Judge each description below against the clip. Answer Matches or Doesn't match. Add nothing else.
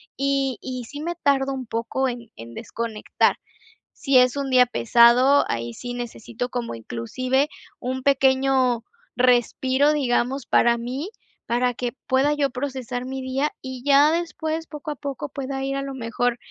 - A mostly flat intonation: Matches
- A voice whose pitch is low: Doesn't match